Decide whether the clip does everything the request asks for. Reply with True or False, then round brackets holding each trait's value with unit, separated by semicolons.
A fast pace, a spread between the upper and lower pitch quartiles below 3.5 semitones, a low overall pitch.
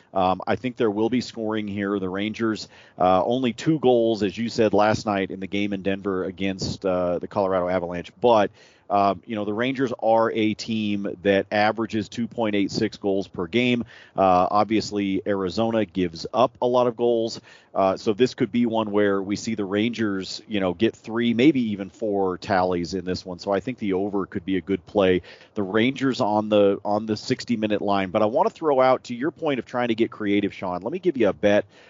True (215 wpm; 2.8 semitones; 105 Hz)